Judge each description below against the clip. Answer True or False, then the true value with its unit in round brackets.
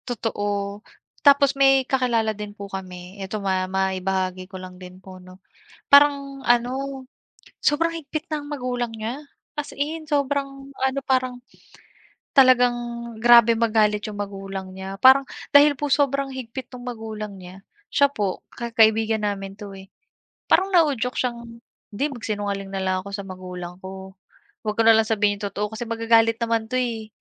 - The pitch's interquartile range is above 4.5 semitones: True (5.1 semitones)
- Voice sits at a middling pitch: False (225 Hz)